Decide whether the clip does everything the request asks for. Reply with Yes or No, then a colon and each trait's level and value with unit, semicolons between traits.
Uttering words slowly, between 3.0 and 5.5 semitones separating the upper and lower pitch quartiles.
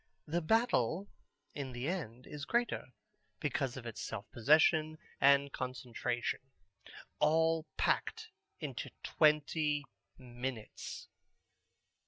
Yes: slow, 95 wpm; average, 4.1 semitones